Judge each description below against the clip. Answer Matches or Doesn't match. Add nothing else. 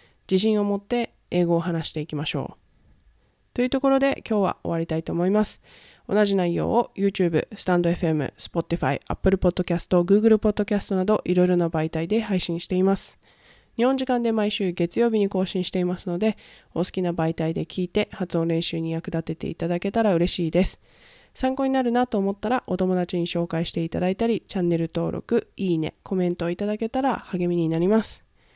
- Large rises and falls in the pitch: Doesn't match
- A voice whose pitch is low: Doesn't match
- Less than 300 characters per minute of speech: Doesn't match